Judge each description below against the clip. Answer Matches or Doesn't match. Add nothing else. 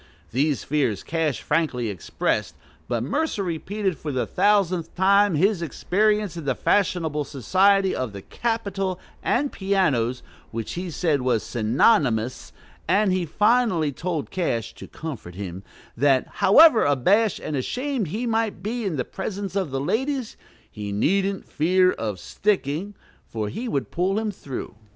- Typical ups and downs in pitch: Doesn't match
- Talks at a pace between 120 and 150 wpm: Matches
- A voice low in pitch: Doesn't match